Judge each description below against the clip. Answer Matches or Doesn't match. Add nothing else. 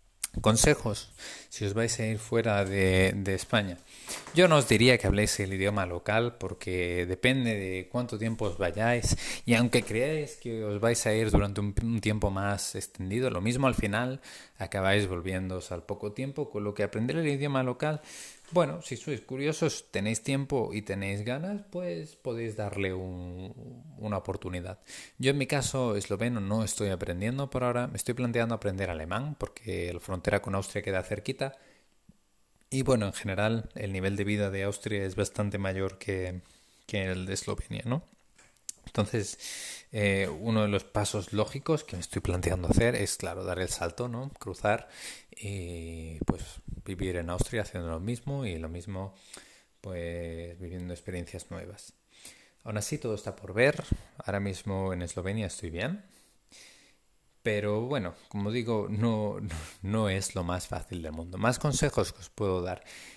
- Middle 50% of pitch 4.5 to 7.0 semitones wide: Doesn't match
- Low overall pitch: Matches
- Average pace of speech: Matches